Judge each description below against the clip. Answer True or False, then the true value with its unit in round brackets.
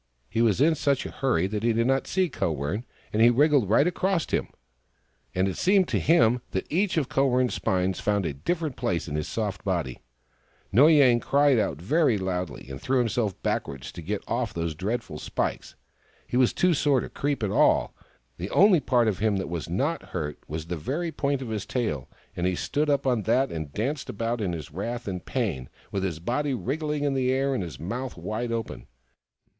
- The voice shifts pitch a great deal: True (7.0 semitones)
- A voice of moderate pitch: False (115 Hz)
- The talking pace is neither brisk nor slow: False (215 wpm)